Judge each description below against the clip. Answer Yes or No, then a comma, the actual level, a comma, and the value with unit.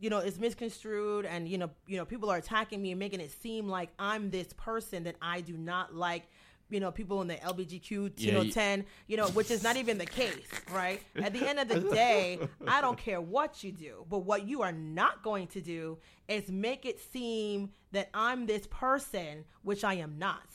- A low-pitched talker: No, high, 200 Hz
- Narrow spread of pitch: No, average, 3.3 semitones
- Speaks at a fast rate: Yes, fast, 220 wpm